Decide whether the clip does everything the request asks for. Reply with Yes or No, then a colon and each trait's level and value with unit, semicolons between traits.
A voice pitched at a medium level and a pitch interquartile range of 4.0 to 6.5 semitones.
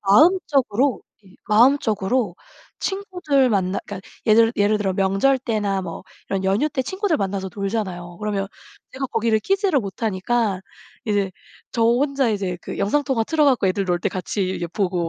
No: high, 210 Hz; wide, 5.4 semitones